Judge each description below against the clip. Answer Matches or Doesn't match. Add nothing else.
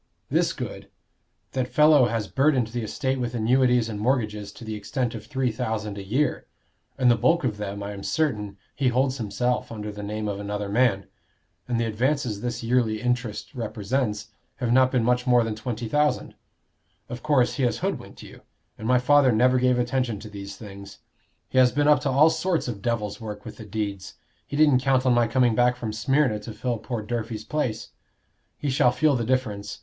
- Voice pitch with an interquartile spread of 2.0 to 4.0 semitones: Matches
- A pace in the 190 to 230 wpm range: Matches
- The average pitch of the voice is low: Matches